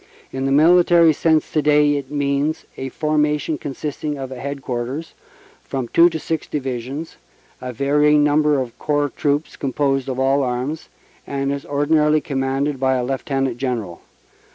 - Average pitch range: No, narrow, 2.1 semitones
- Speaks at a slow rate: No, average, 160 wpm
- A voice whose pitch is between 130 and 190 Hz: Yes, medium, 140 Hz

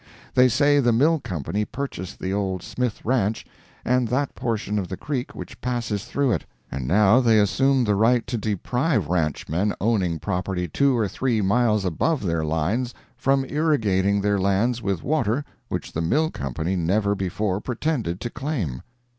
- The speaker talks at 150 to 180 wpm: Yes, average, 165 wpm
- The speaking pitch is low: Yes, low, 105 Hz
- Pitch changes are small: No, average, 5.0 semitones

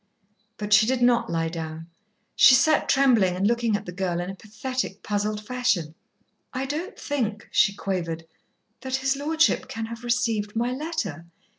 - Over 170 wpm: No, average, 165 wpm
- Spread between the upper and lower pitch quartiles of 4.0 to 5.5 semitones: Yes, average, 5.1 semitones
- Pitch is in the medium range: No, high, 220 Hz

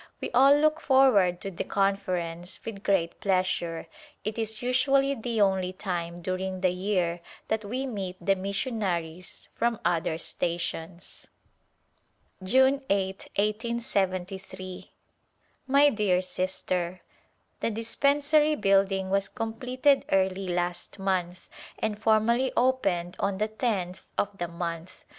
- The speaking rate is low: Yes, slow, 120 wpm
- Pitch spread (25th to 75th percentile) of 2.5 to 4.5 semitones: Yes, average, 4.0 semitones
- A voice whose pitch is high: Yes, high, 195 Hz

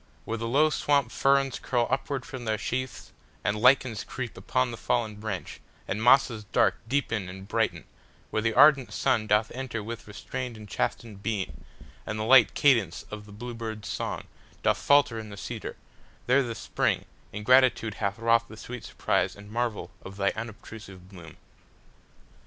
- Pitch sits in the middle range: No, low, 115 Hz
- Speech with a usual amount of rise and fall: Yes, average, 3.3 semitones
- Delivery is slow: No, average, 145 wpm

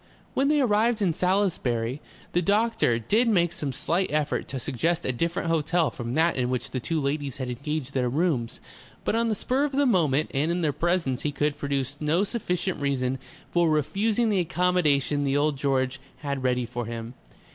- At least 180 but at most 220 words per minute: Yes, average, 190 wpm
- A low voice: No, medium, 150 Hz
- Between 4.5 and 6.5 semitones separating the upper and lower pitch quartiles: Yes, average, 5.3 semitones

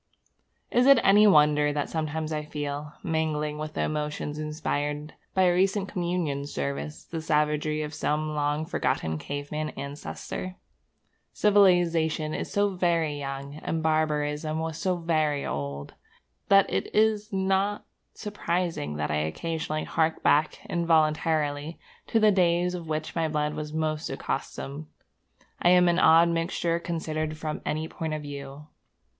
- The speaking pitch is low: No, medium, 155 Hz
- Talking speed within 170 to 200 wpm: No, average, 140 wpm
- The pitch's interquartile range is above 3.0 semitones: No, narrow, 2.4 semitones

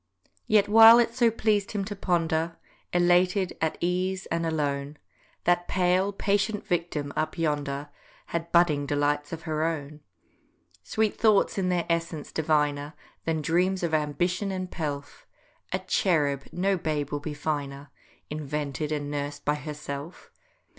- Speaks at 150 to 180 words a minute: No, average, 140 wpm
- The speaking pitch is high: No, medium, 165 Hz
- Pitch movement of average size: Yes, average, 3.8 semitones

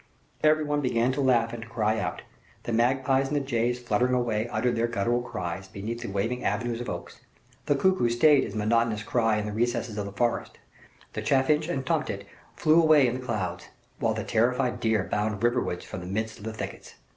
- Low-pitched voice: Yes, low, 120 Hz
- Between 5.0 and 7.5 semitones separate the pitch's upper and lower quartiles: No, average, 3.0 semitones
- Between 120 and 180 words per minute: No, fast, 205 wpm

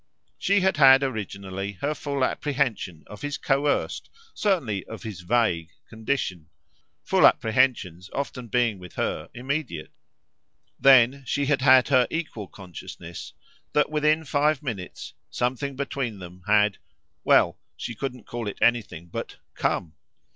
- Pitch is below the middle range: Yes, low, 120 Hz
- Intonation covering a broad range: Yes, wide, 6.0 semitones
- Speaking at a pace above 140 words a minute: No, slow, 135 wpm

